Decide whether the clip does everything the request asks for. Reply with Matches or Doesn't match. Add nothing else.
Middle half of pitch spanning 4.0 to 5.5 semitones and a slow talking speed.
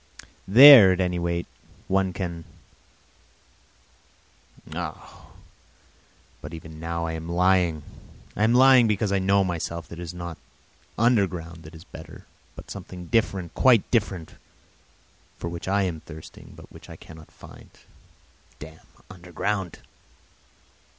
Doesn't match